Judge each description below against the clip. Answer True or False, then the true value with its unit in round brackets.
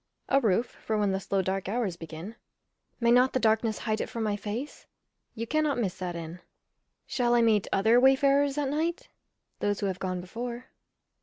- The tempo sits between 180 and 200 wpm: True (185 wpm)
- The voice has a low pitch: False (225 Hz)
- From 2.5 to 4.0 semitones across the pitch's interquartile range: False (4.5 semitones)